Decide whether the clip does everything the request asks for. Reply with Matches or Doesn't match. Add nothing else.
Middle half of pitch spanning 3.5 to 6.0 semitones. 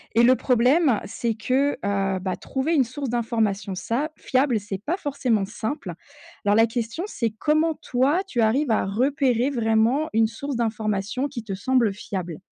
Matches